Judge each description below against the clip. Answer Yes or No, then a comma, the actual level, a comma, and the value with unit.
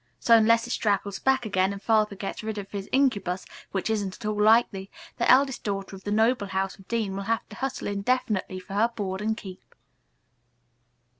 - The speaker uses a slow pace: No, average, 200 wpm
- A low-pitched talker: No, high, 210 Hz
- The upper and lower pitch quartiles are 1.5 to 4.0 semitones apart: Yes, average, 2.7 semitones